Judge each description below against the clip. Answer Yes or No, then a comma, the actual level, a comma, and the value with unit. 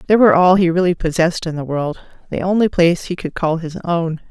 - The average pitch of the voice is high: No, medium, 170 Hz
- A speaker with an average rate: No, fast, 235 wpm